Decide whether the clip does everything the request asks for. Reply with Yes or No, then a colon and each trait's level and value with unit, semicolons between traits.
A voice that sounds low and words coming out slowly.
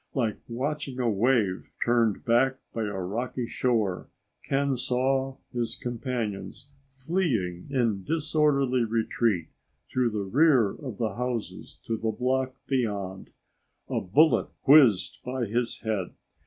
Yes: low, 120 Hz; slow, 125 wpm